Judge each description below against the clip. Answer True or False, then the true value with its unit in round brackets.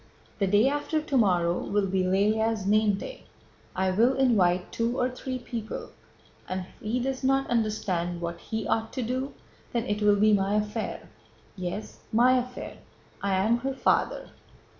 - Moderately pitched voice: False (215 Hz)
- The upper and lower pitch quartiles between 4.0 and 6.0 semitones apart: True (4.6 semitones)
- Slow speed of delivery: False (160 wpm)